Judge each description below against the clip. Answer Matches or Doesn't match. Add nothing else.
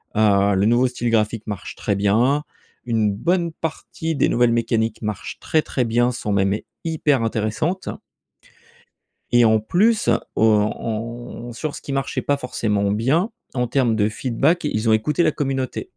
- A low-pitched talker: Matches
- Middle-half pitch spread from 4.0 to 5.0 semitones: Matches